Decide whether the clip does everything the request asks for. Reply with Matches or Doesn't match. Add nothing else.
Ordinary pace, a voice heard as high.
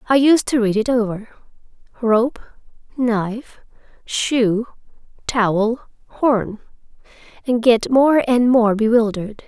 Doesn't match